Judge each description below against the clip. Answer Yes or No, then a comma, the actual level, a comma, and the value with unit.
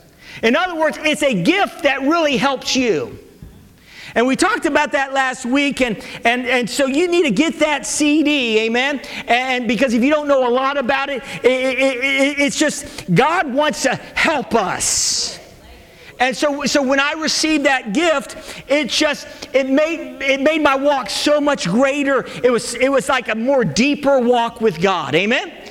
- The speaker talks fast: No, average, 185 wpm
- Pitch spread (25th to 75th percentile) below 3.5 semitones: Yes, average, 2.8 semitones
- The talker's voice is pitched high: Yes, very high, 275 Hz